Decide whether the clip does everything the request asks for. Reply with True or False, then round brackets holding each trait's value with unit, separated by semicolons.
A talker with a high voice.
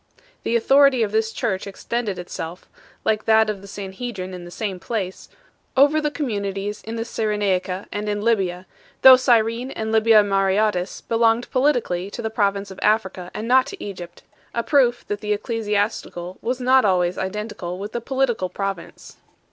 True (210 Hz)